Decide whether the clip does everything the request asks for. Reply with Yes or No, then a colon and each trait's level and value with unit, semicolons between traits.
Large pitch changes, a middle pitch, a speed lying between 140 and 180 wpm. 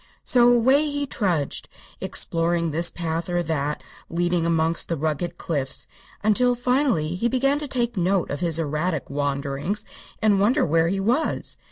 Yes: wide, 6.8 semitones; medium, 175 Hz; average, 155 wpm